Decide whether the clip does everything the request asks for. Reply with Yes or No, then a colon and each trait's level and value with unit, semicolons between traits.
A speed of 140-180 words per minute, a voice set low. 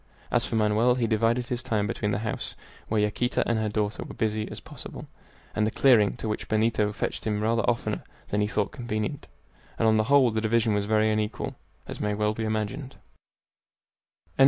No: average, 200 wpm; low, 110 Hz